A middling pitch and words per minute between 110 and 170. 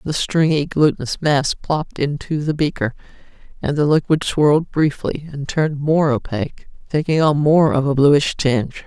Yes: medium, 145 Hz; average, 160 wpm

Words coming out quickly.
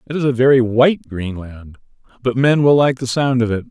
Yes: fast, 225 wpm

